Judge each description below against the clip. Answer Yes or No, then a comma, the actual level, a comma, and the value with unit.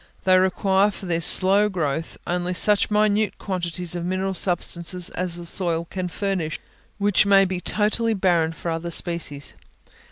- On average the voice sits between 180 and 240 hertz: Yes, medium, 185 Hz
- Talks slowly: No, average, 155 wpm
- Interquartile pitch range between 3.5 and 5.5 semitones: No, narrow, 2.4 semitones